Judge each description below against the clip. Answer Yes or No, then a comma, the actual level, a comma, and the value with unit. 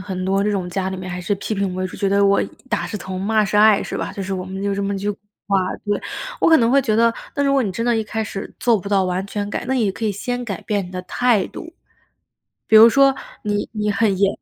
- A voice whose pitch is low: No, high, 205 Hz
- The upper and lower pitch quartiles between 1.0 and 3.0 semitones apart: Yes, narrow, 2.5 semitones